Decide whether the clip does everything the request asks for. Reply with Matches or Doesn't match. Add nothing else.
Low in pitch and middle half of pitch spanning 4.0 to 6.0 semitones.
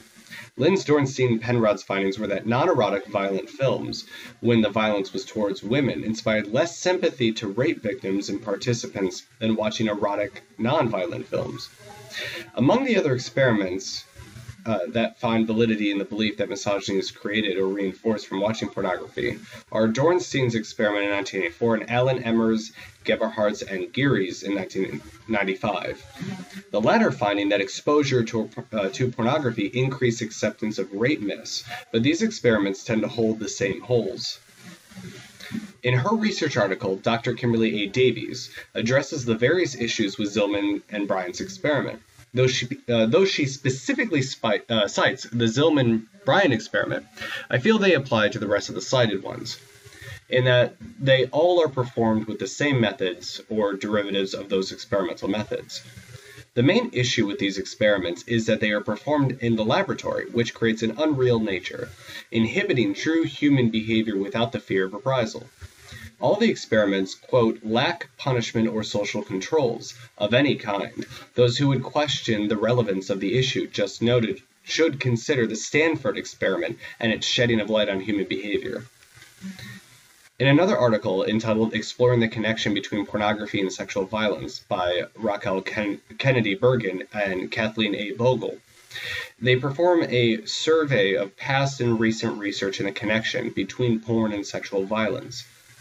Doesn't match